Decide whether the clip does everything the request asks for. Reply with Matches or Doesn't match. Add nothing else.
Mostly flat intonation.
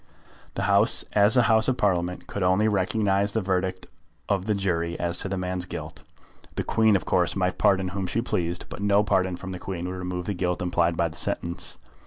Matches